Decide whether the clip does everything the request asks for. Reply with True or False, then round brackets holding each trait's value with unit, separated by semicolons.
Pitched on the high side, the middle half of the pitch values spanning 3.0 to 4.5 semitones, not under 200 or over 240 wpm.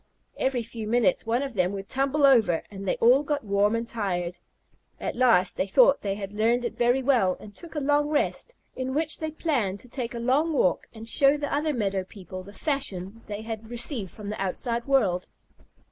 False (235 Hz; 5.4 semitones; 205 wpm)